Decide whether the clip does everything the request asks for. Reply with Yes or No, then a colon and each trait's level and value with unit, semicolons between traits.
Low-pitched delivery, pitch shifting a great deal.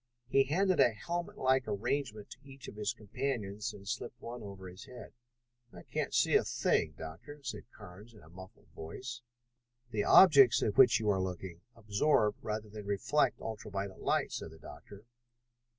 No: low, 105 Hz; average, 4.9 semitones